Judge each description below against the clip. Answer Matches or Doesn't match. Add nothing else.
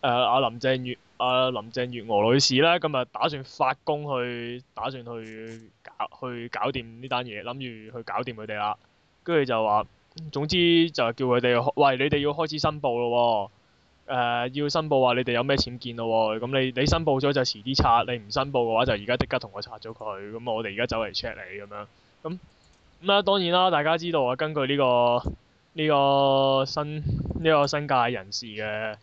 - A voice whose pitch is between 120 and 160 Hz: Matches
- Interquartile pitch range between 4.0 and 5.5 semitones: Doesn't match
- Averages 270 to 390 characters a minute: Matches